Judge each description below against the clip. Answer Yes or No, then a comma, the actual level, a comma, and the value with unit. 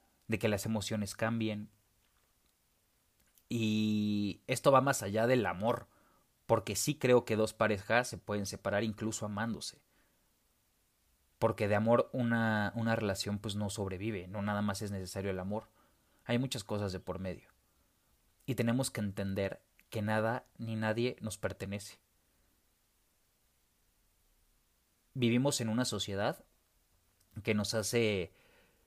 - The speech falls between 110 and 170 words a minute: Yes, average, 130 wpm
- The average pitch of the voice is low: Yes, low, 105 Hz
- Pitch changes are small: Yes, narrow, 2.3 semitones